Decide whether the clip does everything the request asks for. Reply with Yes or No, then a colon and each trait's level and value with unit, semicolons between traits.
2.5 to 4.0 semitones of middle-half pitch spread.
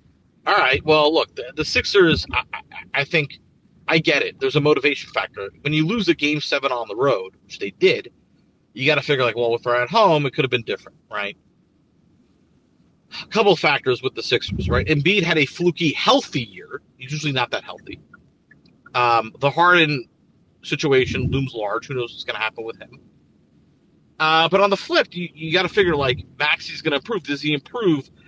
No: average, 4.8 semitones